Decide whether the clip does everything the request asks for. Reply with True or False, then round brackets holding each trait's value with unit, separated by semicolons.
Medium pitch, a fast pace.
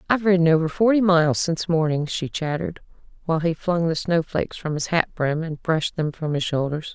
True (165 Hz; 215 wpm)